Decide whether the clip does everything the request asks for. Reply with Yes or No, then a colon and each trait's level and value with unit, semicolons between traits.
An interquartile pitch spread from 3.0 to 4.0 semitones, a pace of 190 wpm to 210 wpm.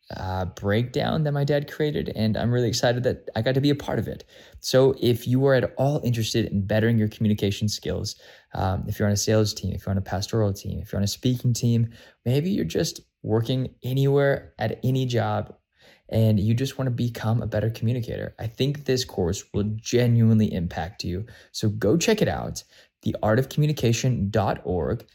Yes: average, 3.6 semitones; average, 195 wpm